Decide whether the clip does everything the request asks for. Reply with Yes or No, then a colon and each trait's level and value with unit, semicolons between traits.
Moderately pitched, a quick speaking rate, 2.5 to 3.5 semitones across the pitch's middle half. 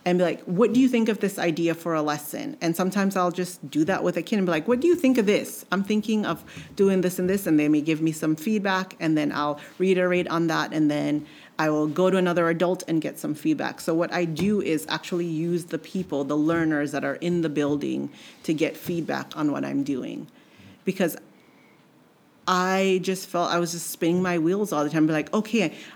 Yes: medium, 175 Hz; fast, 235 wpm; average, 3.2 semitones